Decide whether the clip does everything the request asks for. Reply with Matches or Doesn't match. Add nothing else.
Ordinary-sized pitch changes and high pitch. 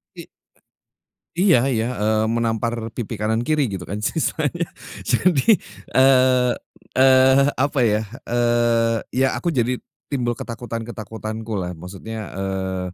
Doesn't match